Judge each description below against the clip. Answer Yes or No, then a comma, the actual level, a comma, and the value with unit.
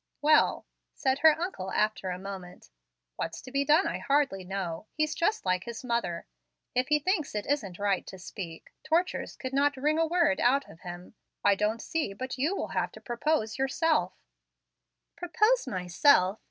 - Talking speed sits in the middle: Yes, average, 180 wpm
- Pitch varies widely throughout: Yes, wide, 7.9 semitones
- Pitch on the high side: Yes, very high, 260 Hz